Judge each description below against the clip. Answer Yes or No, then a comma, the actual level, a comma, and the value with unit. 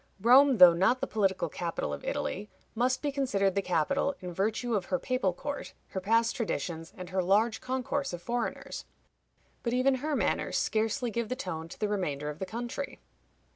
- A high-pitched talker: Yes, high, 220 Hz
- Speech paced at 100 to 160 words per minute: No, average, 185 wpm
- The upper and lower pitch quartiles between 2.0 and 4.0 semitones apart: No, wide, 5.6 semitones